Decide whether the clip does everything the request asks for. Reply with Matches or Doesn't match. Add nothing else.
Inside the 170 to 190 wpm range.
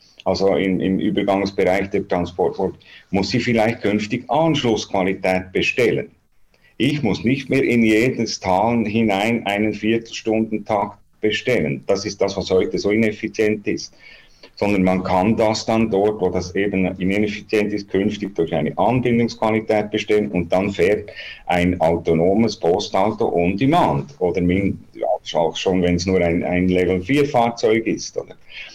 Doesn't match